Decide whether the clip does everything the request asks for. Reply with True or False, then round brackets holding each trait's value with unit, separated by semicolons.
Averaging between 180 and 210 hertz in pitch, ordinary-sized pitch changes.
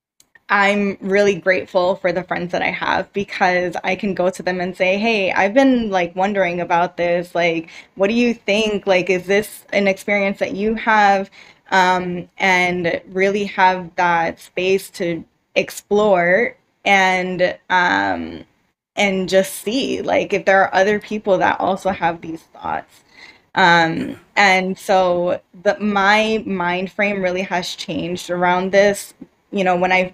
False (190 Hz; 1.8 semitones)